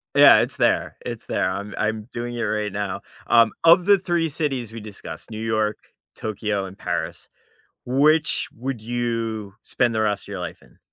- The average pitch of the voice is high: No, low, 110 Hz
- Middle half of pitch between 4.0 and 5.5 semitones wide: No, average, 2.9 semitones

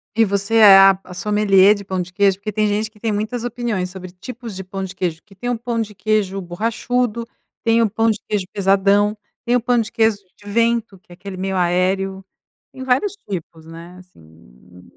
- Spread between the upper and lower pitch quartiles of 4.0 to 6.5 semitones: No, average, 3.3 semitones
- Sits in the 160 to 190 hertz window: No, high, 200 Hz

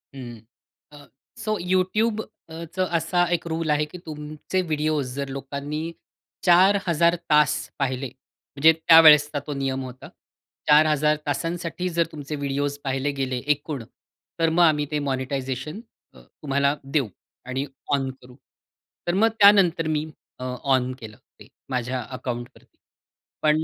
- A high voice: No, medium, 150 Hz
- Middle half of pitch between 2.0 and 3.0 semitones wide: No, average, 3.5 semitones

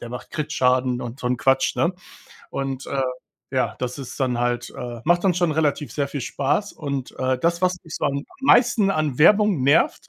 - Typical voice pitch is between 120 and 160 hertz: Yes, medium, 140 Hz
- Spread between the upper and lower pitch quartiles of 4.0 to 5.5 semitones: Yes, average, 4.8 semitones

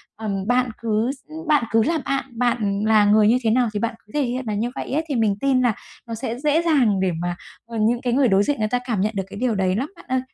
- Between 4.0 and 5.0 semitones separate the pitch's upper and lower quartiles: No, average, 3.4 semitones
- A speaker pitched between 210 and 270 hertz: Yes, high, 230 Hz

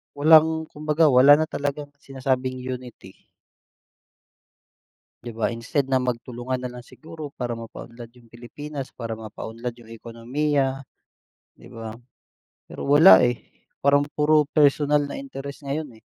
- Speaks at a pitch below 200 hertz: Yes, low, 135 Hz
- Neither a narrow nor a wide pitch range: Yes, average, 3.4 semitones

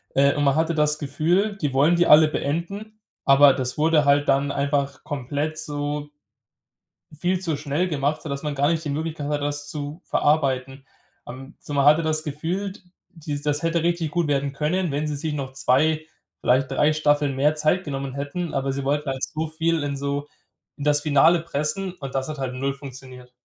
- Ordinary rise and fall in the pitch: No, narrow, 2.2 semitones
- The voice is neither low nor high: Yes, medium, 145 Hz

